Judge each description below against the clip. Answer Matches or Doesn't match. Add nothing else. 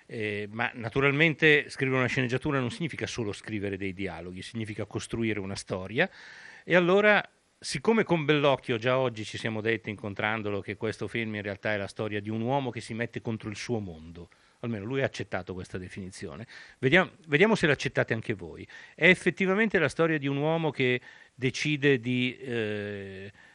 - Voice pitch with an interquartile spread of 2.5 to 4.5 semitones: Doesn't match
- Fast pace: Matches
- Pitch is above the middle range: Doesn't match